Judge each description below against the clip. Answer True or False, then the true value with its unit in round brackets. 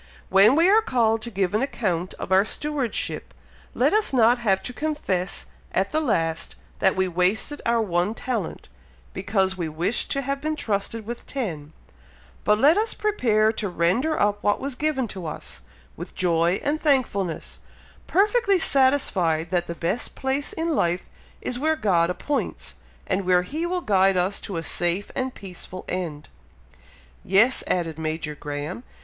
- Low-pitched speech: False (205 Hz)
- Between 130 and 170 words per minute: True (165 wpm)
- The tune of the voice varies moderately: False (7.2 semitones)